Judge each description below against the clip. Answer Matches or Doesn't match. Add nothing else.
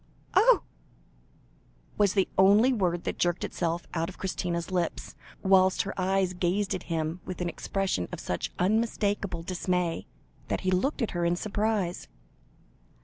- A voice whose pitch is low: Doesn't match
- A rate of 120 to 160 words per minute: Matches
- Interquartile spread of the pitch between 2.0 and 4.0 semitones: Matches